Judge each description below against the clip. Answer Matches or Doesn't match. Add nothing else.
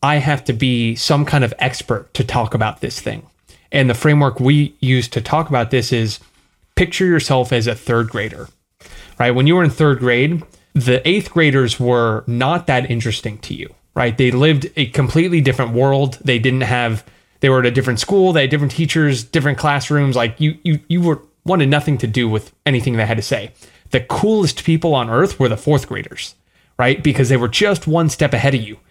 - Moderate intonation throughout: Matches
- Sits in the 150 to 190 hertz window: Doesn't match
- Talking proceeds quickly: Matches